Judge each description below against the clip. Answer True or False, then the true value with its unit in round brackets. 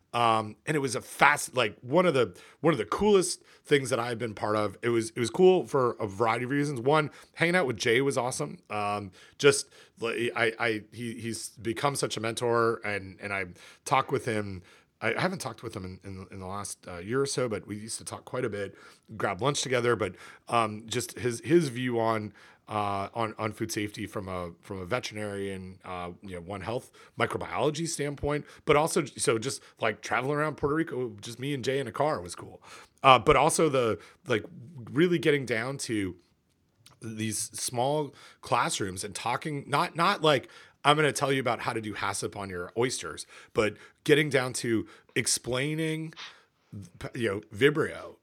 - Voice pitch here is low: True (115 Hz)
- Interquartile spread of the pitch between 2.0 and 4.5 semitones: False (5.4 semitones)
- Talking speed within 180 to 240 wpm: True (200 wpm)